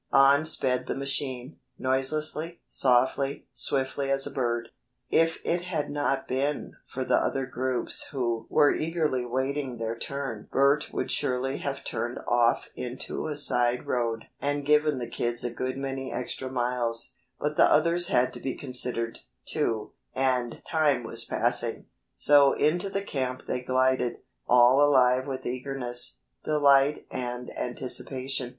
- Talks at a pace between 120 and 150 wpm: Yes, average, 145 wpm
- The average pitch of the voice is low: Yes, low, 130 Hz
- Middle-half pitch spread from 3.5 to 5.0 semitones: No, narrow, 2.6 semitones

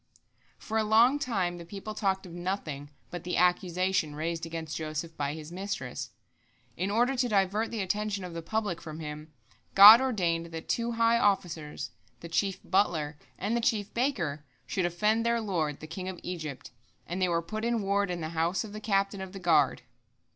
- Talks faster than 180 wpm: Yes, average, 190 wpm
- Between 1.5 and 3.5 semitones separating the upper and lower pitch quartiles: No, average, 4.3 semitones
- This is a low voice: No, medium, 185 Hz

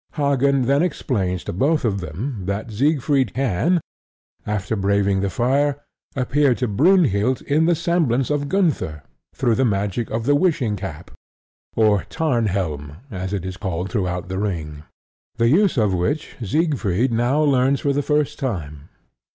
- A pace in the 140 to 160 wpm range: Yes, average, 150 wpm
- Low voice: Yes, low, 120 Hz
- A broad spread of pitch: Yes, wide, 6.8 semitones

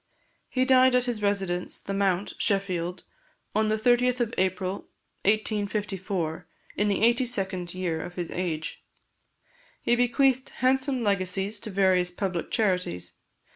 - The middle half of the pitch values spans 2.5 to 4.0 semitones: No, average, 4.4 semitones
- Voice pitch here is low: No, high, 200 Hz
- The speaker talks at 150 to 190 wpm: No, slow, 135 wpm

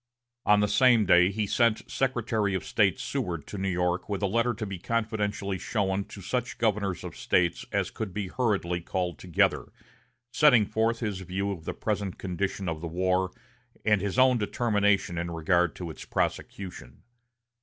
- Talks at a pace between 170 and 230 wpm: Yes, average, 180 wpm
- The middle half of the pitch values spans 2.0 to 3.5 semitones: Yes, average, 3.2 semitones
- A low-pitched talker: Yes, low, 100 Hz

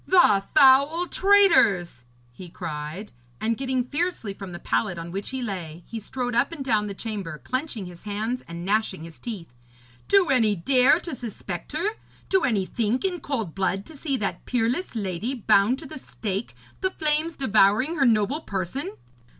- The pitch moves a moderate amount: No, wide, 6.2 semitones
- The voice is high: Yes, high, 225 Hz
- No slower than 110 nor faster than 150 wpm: No, average, 175 wpm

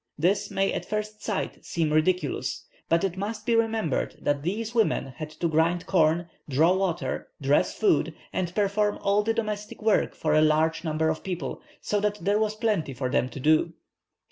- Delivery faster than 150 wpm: Yes, average, 185 wpm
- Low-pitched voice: No, medium, 180 Hz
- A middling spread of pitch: Yes, average, 5.0 semitones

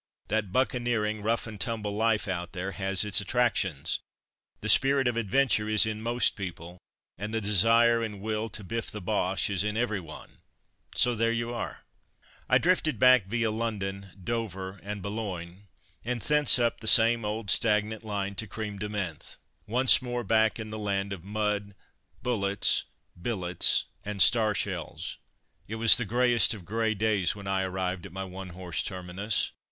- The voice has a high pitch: No, low, 105 Hz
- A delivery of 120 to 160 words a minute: No, average, 170 wpm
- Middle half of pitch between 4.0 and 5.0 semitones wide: No, average, 2.9 semitones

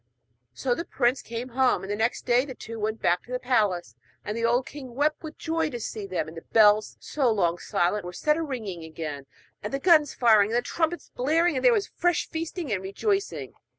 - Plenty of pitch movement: Yes, wide, 6.4 semitones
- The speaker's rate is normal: No, fast, 225 wpm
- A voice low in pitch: No, high, 240 Hz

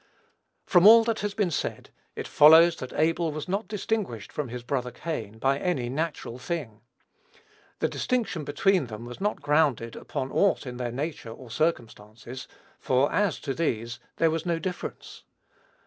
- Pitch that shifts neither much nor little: No, wide, 6.3 semitones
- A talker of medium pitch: Yes, medium, 150 Hz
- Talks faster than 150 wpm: Yes, average, 165 wpm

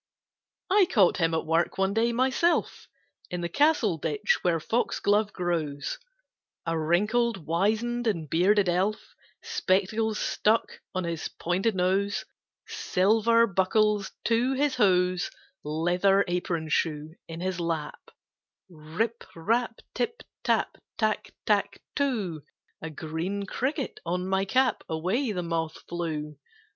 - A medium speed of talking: No, slow, 125 wpm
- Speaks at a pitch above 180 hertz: Yes, high, 190 Hz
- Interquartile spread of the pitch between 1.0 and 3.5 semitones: No, average, 5.2 semitones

